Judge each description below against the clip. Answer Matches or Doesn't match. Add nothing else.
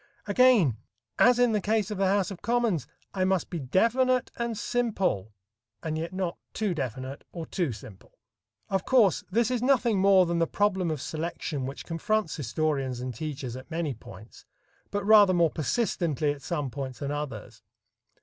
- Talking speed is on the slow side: Doesn't match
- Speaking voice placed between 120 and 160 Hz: Doesn't match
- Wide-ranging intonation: Matches